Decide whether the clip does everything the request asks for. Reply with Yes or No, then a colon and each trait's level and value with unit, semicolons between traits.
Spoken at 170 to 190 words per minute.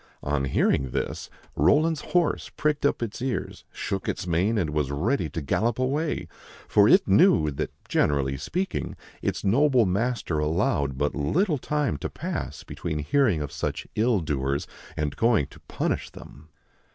No: average, 155 wpm